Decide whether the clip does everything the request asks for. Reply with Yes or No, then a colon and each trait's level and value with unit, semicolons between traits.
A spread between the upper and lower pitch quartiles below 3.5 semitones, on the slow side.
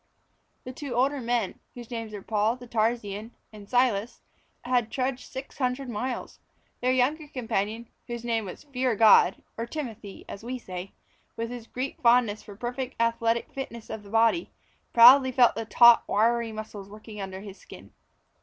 No: average, 2.7 semitones; average, 165 wpm